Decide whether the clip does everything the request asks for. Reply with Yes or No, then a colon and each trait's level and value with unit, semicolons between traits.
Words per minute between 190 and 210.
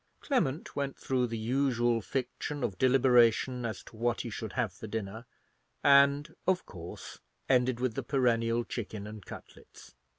No: average, 155 wpm